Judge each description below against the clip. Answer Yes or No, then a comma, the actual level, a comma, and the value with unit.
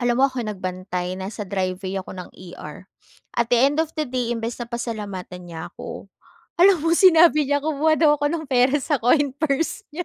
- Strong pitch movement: Yes, wide, 7.7 semitones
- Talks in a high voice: Yes, high, 245 Hz